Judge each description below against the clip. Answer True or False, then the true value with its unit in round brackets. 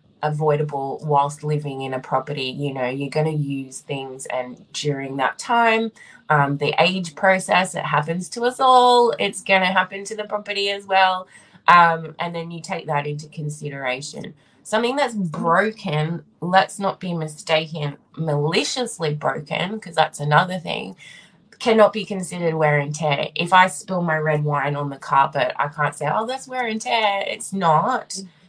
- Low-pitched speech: False (165 Hz)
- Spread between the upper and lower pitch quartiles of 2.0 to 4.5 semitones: False (5.0 semitones)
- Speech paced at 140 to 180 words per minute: True (170 wpm)